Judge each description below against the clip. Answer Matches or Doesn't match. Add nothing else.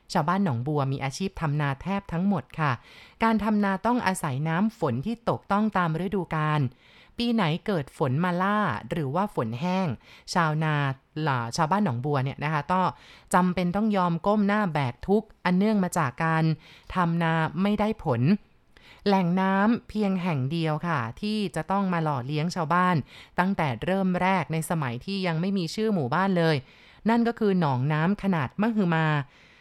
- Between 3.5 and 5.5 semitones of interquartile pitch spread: Matches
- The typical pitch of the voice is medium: Matches